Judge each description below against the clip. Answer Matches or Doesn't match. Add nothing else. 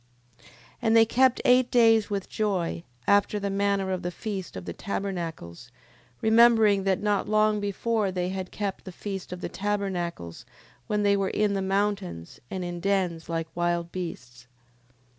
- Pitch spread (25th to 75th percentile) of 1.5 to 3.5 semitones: Matches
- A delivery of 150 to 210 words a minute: Matches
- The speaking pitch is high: Matches